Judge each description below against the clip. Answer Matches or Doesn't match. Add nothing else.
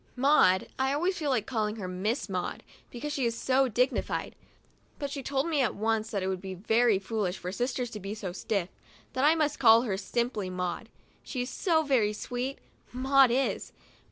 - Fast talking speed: Matches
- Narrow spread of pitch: Doesn't match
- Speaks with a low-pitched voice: Doesn't match